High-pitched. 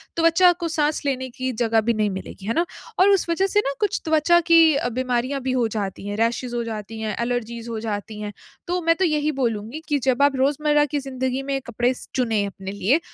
Yes: very high, 255 Hz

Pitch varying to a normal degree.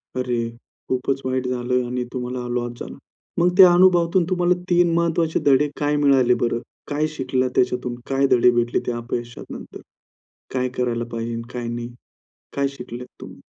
Yes: average, 3.3 semitones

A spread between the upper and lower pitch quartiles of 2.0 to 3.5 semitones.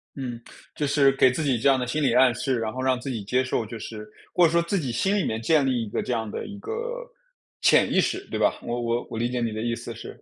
No: average, 4.0 semitones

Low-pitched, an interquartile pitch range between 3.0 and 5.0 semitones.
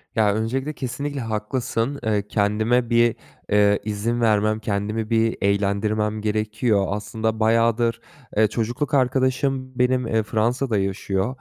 No: low, 110 Hz; narrow, 2.5 semitones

